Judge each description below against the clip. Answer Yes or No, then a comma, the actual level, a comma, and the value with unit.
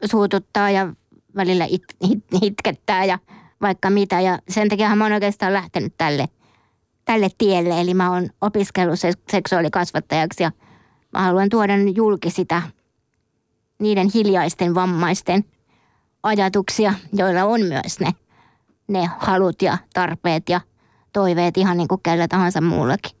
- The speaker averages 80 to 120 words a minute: No, average, 130 wpm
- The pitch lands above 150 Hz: Yes, medium, 185 Hz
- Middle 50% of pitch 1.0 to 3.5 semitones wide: Yes, narrow, 2.4 semitones